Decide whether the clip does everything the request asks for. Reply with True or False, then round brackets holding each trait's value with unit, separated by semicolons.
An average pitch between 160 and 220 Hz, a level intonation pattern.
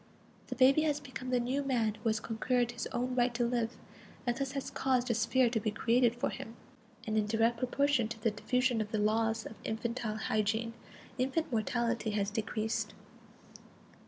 False (235 Hz; 2.3 semitones)